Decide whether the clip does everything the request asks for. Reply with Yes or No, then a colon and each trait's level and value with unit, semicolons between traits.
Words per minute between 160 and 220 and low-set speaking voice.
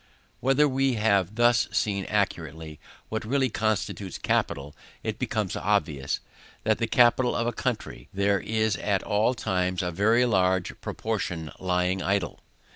No: average, 145 wpm; low, 105 Hz